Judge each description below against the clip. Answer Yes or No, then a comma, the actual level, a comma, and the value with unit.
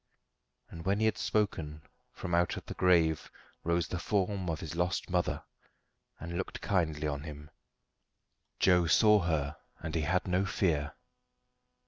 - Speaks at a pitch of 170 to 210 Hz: No, very low, 85 Hz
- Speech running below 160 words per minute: Yes, average, 145 wpm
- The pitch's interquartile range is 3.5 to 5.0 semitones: No, average, 2.8 semitones